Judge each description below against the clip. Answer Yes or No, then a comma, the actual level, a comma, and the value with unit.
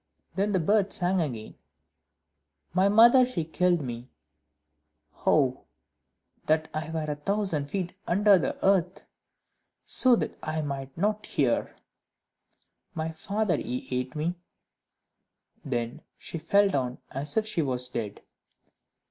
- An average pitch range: No, wide, 6.1 semitones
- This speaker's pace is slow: Yes, slow, 125 wpm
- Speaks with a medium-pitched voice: Yes, medium, 160 Hz